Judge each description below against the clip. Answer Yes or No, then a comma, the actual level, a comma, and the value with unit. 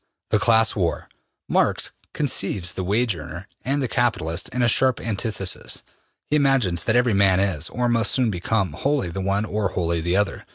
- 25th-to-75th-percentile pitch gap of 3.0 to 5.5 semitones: Yes, average, 4.8 semitones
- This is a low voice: Yes, low, 105 Hz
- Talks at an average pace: Yes, average, 180 wpm